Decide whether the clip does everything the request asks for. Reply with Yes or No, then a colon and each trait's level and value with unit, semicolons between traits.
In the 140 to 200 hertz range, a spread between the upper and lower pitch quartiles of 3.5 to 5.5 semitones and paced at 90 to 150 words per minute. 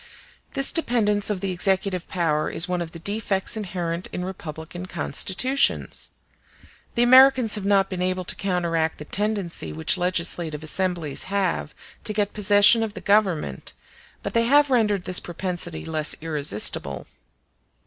Yes: medium, 185 Hz; average, 3.8 semitones; average, 145 wpm